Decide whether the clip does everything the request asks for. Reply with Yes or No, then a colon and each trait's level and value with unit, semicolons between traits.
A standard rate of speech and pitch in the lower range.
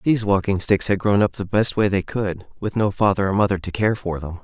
No: fast, 270 wpm; low, 100 Hz